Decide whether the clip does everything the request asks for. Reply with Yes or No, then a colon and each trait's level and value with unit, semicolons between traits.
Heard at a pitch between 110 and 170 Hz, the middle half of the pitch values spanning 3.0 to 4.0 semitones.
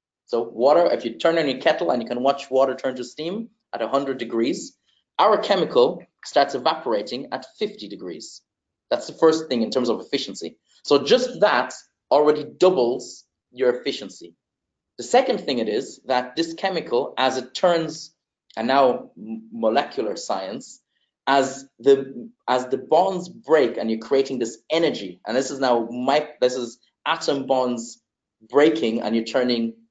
No: low, 135 Hz; average, 4.8 semitones